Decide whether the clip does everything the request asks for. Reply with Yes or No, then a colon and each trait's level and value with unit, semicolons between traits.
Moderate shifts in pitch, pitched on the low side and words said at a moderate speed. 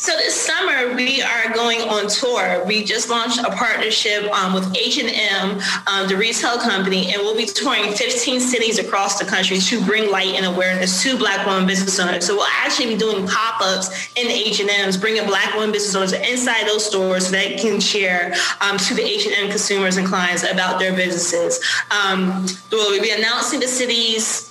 No: average, 3.0 semitones; high, 205 Hz; average, 190 wpm